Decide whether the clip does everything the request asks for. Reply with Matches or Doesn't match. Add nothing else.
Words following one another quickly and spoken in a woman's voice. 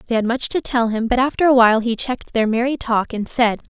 Matches